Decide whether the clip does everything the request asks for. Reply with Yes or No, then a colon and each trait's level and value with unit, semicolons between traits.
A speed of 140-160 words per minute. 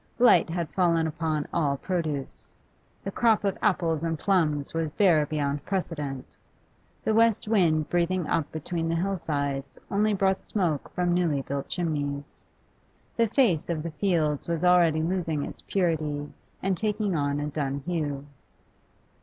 Yes: average, 150 wpm